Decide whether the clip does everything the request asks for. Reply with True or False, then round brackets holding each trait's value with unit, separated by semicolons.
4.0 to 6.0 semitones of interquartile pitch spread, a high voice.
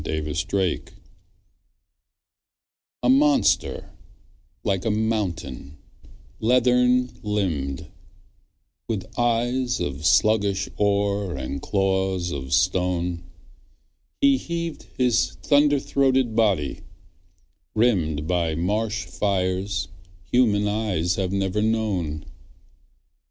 False (4.8 semitones; 100 Hz)